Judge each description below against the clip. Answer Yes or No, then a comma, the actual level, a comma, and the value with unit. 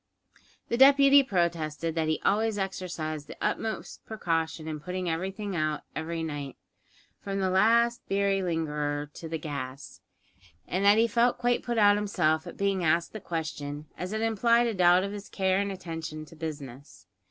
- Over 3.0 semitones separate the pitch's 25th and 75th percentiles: Yes, average, 4.7 semitones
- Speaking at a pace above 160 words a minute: Yes, average, 170 wpm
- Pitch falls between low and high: Yes, medium, 180 Hz